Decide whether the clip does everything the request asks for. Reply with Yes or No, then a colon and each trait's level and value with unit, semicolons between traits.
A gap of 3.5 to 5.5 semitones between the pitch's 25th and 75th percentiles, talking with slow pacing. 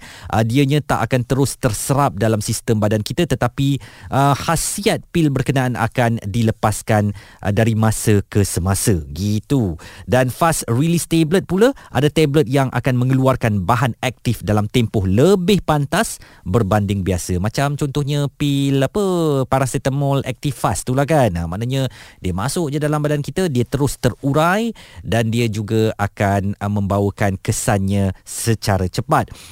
No: average, 5.2 semitones; average, 140 wpm